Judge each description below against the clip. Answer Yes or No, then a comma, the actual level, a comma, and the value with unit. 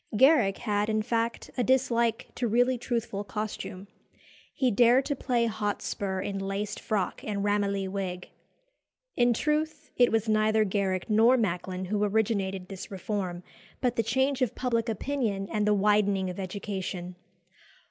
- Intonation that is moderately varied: Yes, average, 3.3 semitones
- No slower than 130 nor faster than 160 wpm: Yes, average, 145 wpm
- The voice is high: Yes, high, 210 Hz